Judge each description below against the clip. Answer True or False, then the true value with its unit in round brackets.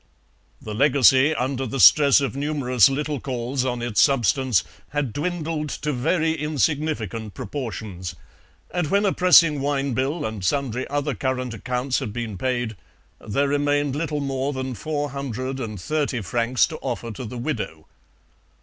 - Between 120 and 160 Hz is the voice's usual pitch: True (135 Hz)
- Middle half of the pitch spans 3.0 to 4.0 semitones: True (3.4 semitones)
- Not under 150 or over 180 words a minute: False (140 wpm)